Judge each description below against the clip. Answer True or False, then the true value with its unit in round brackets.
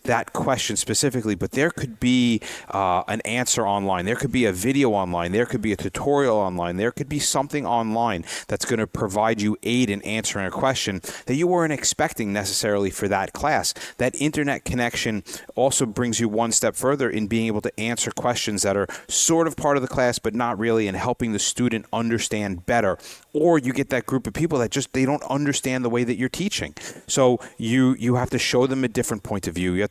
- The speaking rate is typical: False (220 wpm)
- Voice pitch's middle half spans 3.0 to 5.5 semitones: True (3.7 semitones)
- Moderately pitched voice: False (120 Hz)